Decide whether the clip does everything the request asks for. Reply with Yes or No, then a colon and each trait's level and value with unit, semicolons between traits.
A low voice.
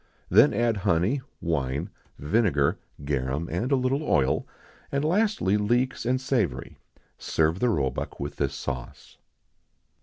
Yes: very low, 95 Hz